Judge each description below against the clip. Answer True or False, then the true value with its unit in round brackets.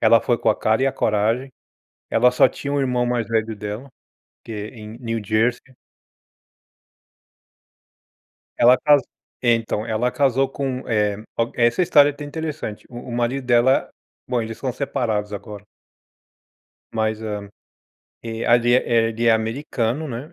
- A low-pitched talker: True (120 Hz)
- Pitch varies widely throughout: False (2.9 semitones)